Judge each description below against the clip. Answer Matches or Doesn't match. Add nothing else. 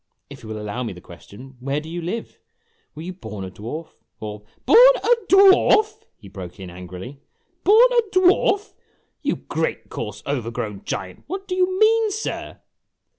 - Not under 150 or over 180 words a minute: Matches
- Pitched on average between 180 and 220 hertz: Doesn't match